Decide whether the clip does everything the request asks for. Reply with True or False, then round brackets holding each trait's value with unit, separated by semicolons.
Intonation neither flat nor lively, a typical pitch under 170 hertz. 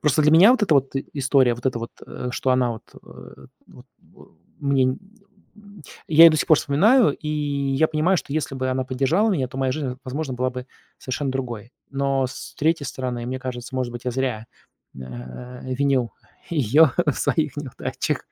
True (3.2 semitones; 135 Hz)